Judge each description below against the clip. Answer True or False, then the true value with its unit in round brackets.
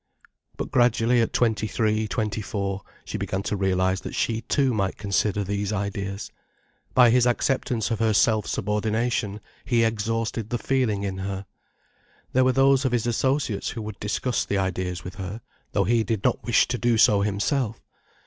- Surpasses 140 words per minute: True (175 wpm)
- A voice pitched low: True (110 Hz)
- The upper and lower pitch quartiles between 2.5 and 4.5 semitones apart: True (3.1 semitones)